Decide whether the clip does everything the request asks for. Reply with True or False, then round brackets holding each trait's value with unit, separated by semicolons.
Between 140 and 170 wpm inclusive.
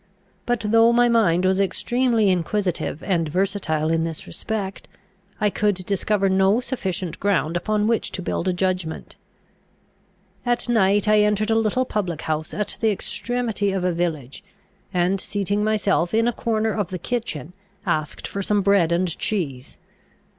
True (155 wpm)